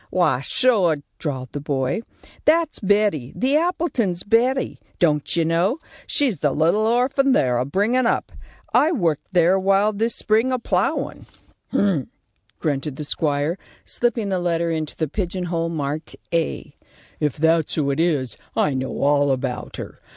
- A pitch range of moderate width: No, wide, 7.0 semitones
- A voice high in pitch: No, medium, 170 Hz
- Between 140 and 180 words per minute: Yes, average, 160 wpm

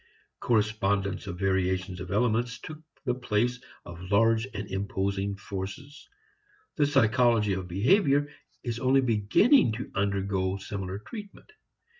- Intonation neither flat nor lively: Yes, average, 4.2 semitones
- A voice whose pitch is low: Yes, low, 105 Hz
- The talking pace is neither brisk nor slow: No, slow, 120 wpm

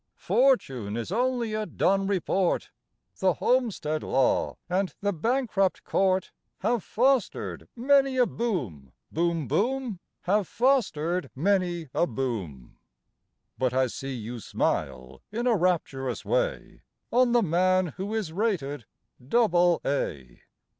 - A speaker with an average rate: No, slow, 120 wpm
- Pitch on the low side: No, medium, 185 Hz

